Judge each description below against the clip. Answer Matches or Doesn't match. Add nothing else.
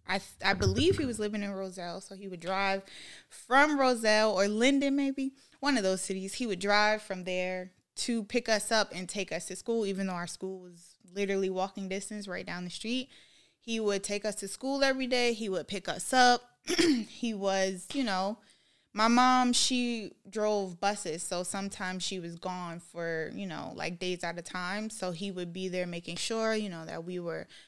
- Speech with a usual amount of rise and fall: Matches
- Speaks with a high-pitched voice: Matches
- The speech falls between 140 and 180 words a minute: Doesn't match